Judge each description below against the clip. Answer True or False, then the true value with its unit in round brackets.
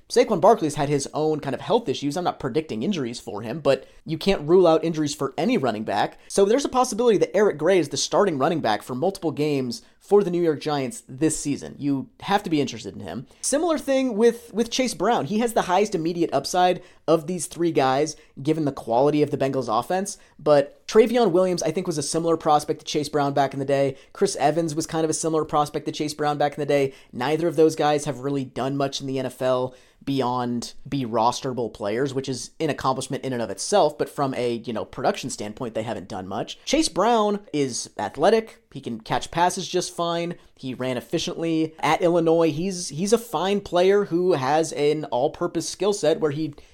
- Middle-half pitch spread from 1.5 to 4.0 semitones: False (4.6 semitones)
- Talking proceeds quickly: True (220 wpm)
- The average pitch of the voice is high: False (155 Hz)